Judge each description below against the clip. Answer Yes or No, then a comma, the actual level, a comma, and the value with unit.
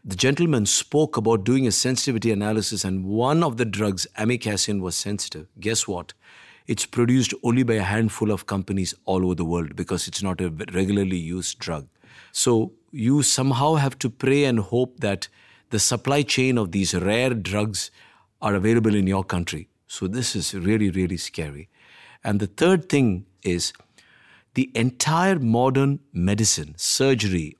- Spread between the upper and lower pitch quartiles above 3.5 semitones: Yes, average, 5.1 semitones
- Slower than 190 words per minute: Yes, average, 160 wpm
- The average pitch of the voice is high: No, low, 110 Hz